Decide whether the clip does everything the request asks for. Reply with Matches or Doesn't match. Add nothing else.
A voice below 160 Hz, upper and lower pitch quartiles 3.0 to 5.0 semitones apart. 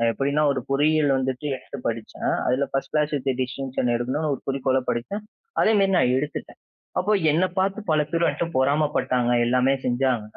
Matches